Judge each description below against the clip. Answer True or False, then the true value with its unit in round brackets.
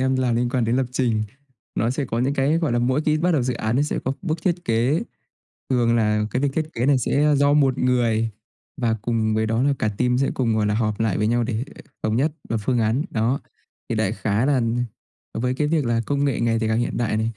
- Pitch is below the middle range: True (120 Hz)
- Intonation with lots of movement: False (3.3 semitones)